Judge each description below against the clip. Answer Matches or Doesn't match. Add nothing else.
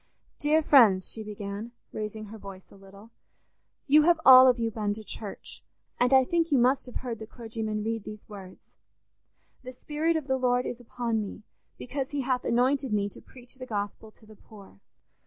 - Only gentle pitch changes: Doesn't match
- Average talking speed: Matches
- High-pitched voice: Matches